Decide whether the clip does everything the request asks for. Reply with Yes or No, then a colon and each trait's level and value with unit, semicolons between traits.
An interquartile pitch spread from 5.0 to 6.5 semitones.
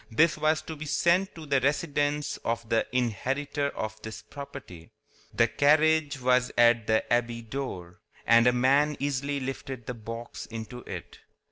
No: average, 3.8 semitones